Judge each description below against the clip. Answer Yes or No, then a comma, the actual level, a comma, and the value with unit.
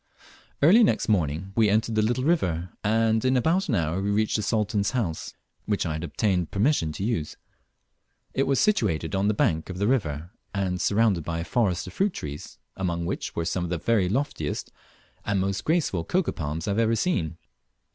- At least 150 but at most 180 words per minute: No, average, 200 wpm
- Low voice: Yes, low, 100 Hz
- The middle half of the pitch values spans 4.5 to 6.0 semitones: Yes, average, 5.2 semitones